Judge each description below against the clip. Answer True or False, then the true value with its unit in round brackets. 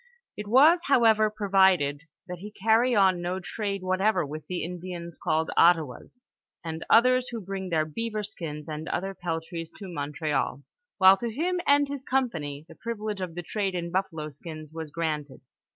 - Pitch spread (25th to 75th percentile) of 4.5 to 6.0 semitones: True (5.0 semitones)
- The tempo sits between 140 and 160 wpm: False (175 wpm)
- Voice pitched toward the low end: False (185 Hz)